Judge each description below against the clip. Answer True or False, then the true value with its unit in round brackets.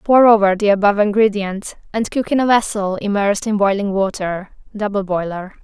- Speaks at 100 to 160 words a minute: False (170 wpm)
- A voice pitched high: True (205 Hz)